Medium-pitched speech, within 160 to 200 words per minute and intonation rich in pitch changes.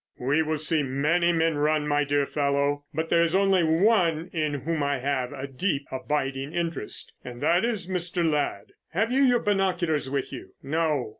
No: medium, 155 Hz; average, 180 wpm; average, 3.5 semitones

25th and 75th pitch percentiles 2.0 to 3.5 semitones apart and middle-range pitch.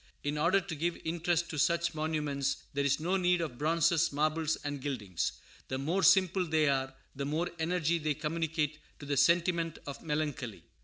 Yes: average, 2.9 semitones; medium, 155 Hz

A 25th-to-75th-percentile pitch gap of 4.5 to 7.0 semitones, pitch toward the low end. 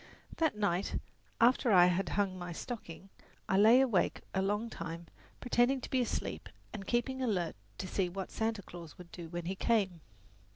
No: average, 4.8 semitones; high, 195 Hz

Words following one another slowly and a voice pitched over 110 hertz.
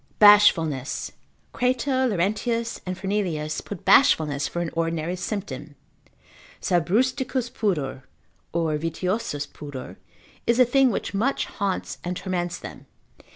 Yes: slow, 110 wpm; medium, 185 Hz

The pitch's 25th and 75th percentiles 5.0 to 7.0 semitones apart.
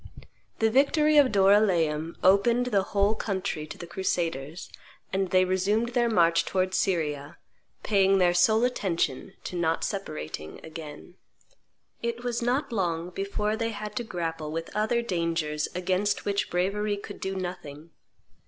No: average, 4.1 semitones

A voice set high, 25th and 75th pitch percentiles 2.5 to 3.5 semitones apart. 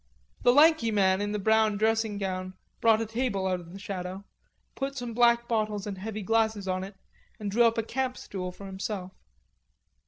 Yes: high, 210 Hz; average, 2.9 semitones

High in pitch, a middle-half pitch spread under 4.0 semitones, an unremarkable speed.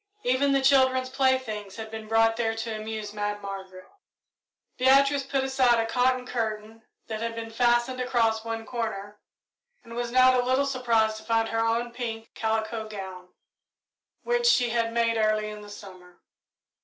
Yes: high, 230 Hz; average, 2.7 semitones; average, 165 wpm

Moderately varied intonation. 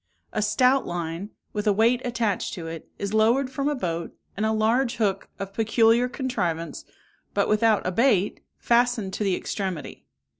Yes: average, 3.9 semitones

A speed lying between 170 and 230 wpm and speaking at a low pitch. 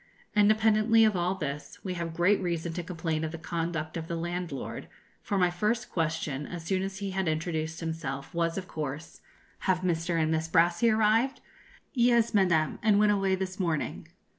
No: average, 180 wpm; medium, 175 Hz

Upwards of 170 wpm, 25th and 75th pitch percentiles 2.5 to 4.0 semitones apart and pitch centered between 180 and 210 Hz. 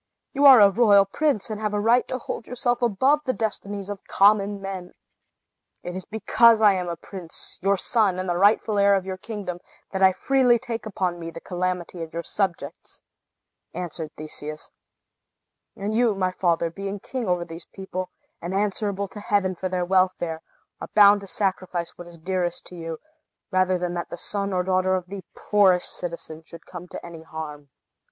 Yes: average, 190 wpm; average, 2.8 semitones; high, 190 Hz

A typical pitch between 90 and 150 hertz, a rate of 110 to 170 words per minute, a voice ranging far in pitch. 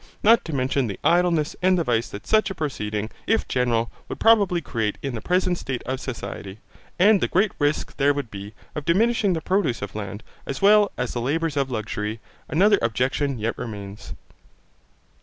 No: medium, 140 Hz; average, 185 wpm; wide, 8.1 semitones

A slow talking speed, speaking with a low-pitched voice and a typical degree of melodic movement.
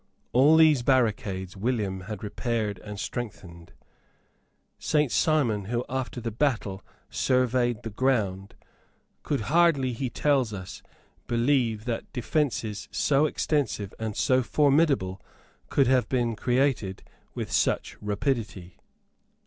Yes: slow, 115 wpm; low, 120 Hz; average, 4.5 semitones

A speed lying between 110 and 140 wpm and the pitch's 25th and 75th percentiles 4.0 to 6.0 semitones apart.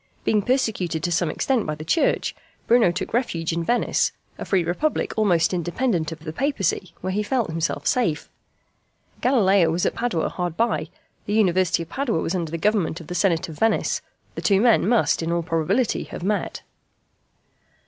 No: average, 180 wpm; average, 5.2 semitones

